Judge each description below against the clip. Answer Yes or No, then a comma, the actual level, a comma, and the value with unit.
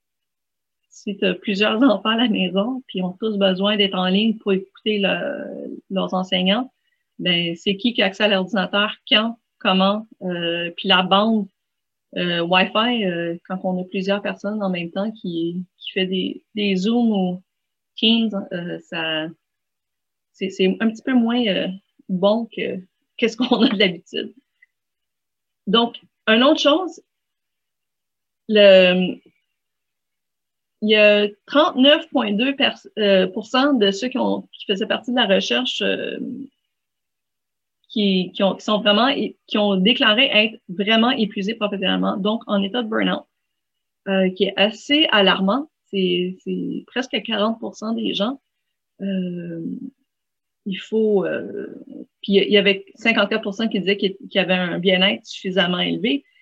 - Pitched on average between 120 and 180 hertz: No, high, 205 Hz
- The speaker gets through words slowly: Yes, slow, 140 wpm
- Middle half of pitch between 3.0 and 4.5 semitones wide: Yes, average, 3.7 semitones